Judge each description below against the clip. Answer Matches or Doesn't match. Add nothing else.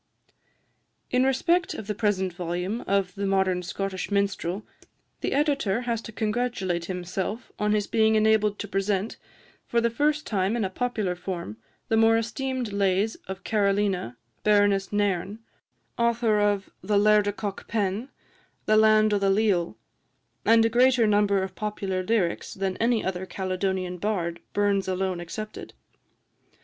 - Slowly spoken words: Doesn't match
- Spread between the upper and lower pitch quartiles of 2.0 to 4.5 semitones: Matches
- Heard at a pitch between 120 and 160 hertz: Doesn't match